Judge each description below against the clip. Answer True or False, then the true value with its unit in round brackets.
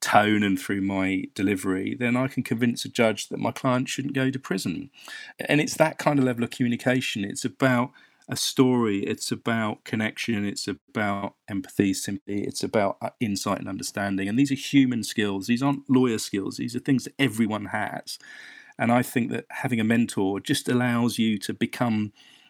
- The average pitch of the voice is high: False (115 Hz)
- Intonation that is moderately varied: True (4.0 semitones)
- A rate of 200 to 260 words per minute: False (185 wpm)